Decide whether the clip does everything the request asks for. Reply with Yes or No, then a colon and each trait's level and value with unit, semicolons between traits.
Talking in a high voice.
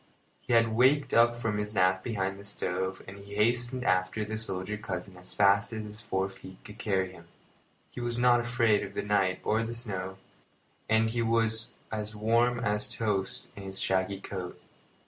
No: low, 105 Hz